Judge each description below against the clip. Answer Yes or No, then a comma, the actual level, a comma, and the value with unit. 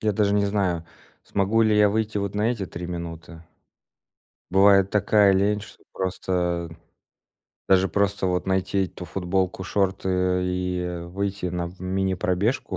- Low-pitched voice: Yes, very low, 95 Hz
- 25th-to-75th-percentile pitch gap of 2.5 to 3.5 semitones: No, narrow, 2.0 semitones